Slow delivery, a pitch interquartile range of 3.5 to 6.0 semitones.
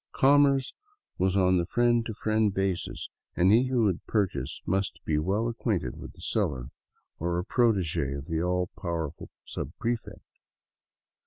No: average, 150 wpm; average, 5.1 semitones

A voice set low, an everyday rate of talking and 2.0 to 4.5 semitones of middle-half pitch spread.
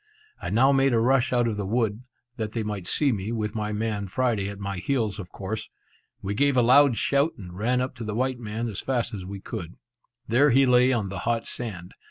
No: low, 115 Hz; fast, 235 wpm; average, 3.7 semitones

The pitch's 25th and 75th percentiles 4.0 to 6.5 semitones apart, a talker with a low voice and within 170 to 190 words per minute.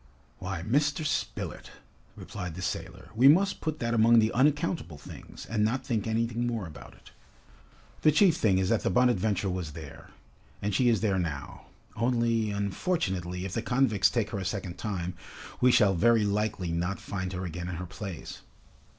Yes: average, 4.5 semitones; low, 105 Hz; average, 175 wpm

